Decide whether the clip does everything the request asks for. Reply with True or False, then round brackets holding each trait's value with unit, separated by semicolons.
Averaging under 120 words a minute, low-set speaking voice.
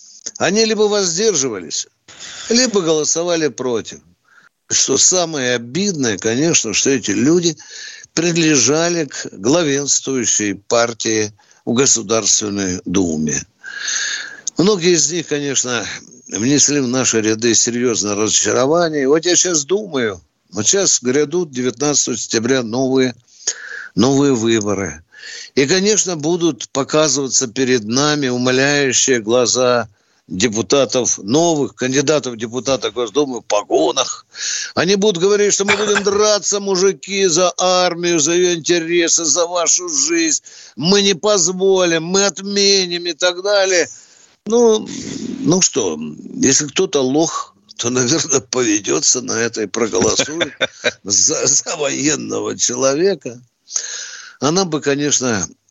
False (110 wpm; 150 Hz)